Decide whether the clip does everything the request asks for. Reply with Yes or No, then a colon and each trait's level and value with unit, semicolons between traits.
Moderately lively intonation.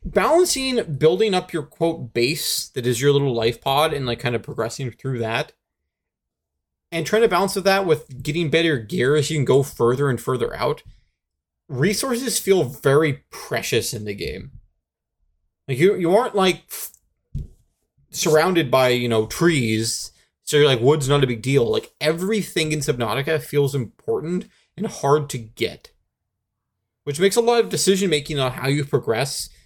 No: wide, 6.5 semitones